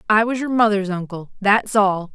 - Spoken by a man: No, female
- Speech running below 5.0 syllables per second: Yes, 4.8 syllables/s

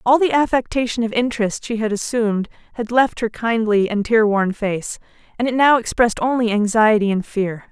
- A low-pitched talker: No, high, 225 Hz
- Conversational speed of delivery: Yes, average, 185 wpm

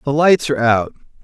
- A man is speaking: Yes, male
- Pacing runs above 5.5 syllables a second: Yes, 5.9 syllables/s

